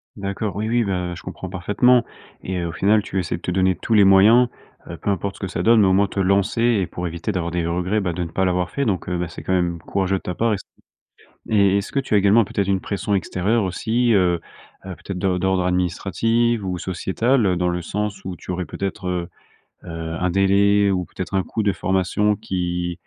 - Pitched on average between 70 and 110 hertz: Yes, very low, 95 Hz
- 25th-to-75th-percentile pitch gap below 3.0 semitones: Yes, narrow, 2.4 semitones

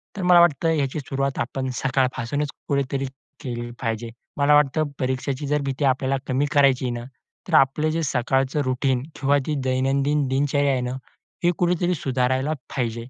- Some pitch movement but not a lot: No, narrow, 2.0 semitones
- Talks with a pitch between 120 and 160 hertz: Yes, low, 135 Hz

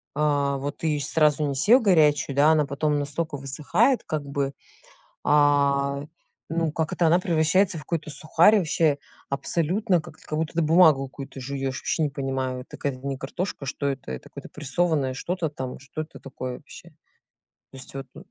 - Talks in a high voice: No, medium, 145 Hz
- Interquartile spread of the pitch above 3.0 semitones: No, average, 2.7 semitones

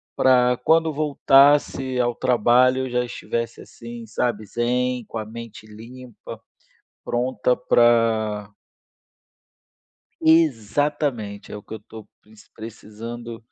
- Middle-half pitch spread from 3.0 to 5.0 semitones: No, narrow, 2.4 semitones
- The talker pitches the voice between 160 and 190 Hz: No, low, 120 Hz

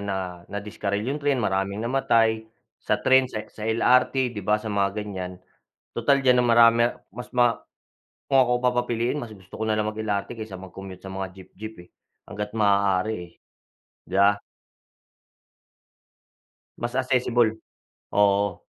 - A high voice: No, low, 110 Hz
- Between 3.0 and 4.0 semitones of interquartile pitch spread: Yes, average, 3.4 semitones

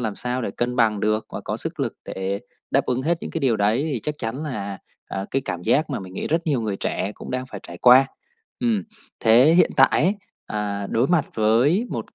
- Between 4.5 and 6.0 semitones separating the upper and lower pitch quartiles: Yes, average, 5.2 semitones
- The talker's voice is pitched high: No, low, 125 Hz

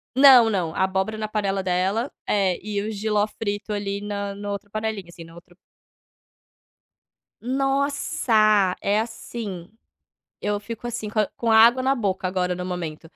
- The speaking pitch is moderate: No, high, 205 Hz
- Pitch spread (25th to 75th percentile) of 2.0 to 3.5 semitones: Yes, average, 2.7 semitones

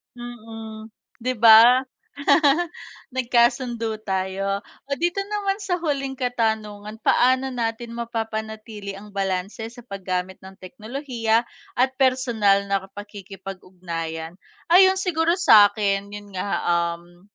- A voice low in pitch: No, high, 220 Hz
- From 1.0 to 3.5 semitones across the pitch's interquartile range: No, average, 4.2 semitones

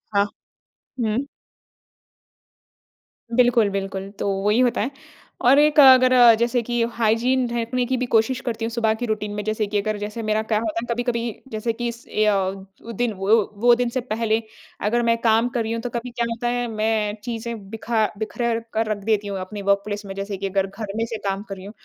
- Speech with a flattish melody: Yes, narrow, 2.3 semitones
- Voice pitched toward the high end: Yes, high, 225 Hz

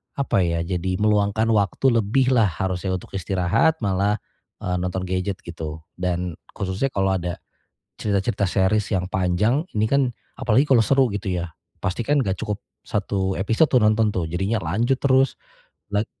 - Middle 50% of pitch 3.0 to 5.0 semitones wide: Yes, average, 3.7 semitones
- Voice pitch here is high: No, low, 100 Hz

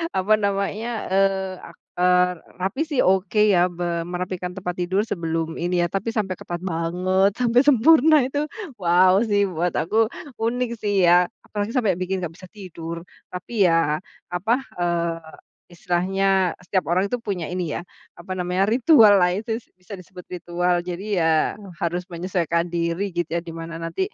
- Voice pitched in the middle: Yes, medium, 180 Hz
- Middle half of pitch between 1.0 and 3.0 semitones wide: Yes, narrow, 2.6 semitones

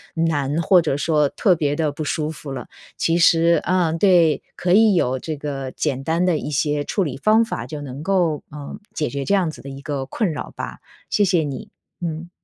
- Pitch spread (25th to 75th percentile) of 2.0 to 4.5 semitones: Yes, average, 3.4 semitones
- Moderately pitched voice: Yes, medium, 155 Hz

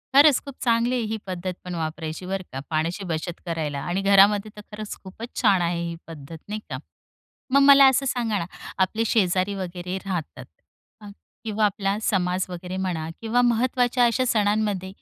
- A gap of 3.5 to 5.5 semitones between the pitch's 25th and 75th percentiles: Yes, average, 4.2 semitones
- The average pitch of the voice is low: No, high, 195 Hz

